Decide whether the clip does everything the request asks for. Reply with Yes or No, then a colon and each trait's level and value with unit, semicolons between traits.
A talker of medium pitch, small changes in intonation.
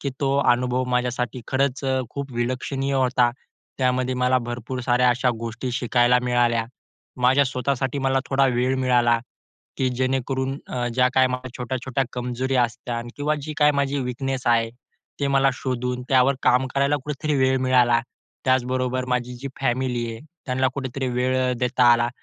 No: low, 130 Hz; narrow, 1.4 semitones